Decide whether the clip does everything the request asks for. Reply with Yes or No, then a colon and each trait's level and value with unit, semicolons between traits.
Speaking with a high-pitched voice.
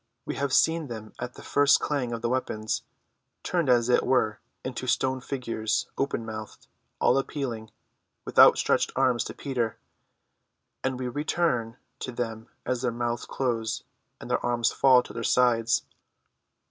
No: low, 125 Hz